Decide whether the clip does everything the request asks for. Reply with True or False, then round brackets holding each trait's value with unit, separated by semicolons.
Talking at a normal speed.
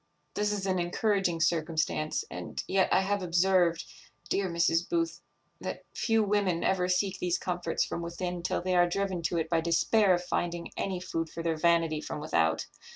True (180 wpm)